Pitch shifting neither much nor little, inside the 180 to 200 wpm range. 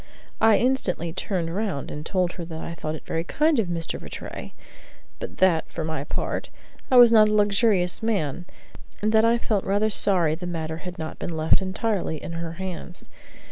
Yes: average, 4.5 semitones; average, 190 wpm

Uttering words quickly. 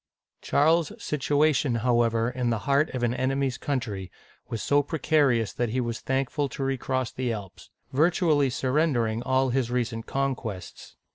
No: average, 155 wpm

